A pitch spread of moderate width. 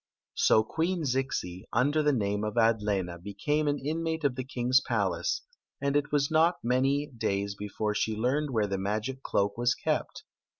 No: wide, 5.8 semitones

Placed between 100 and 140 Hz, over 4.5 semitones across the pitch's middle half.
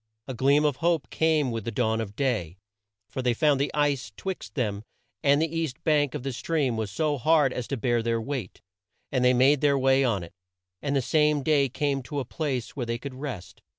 No: low, 135 Hz; average, 3.8 semitones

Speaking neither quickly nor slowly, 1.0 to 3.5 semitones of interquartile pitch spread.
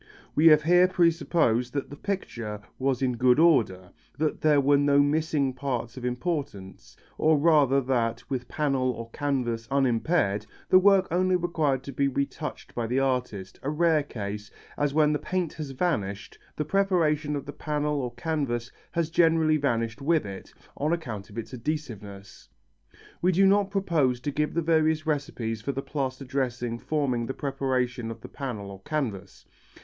No: average, 170 wpm; average, 4.6 semitones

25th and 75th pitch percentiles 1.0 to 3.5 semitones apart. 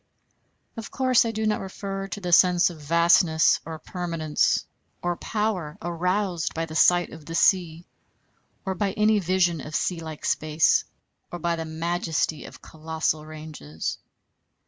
Yes: average, 2.9 semitones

